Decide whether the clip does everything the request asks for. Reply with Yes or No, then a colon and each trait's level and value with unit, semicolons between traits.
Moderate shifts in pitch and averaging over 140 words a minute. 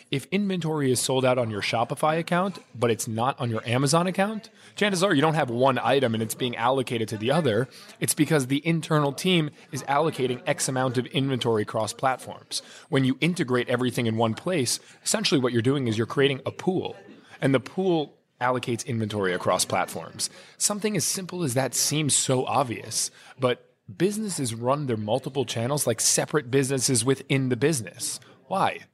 Yes: average, 4.3 semitones; average, 180 wpm